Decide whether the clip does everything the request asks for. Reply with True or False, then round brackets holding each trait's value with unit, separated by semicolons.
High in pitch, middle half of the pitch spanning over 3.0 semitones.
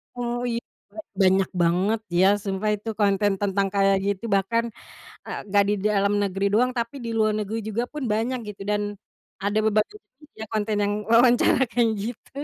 False (210 Hz; 2.6 semitones)